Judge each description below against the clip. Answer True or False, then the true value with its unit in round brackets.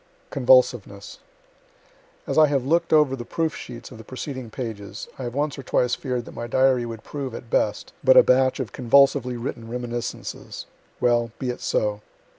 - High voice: False (125 Hz)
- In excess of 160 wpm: True (180 wpm)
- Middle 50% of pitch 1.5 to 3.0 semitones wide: True (2.7 semitones)